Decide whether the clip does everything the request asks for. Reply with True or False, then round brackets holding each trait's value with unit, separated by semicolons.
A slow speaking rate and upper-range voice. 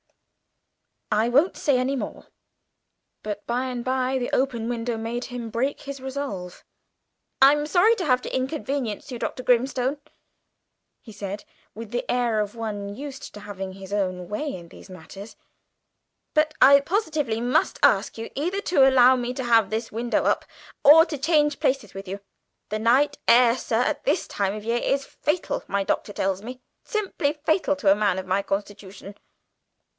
False (170 wpm; 245 Hz)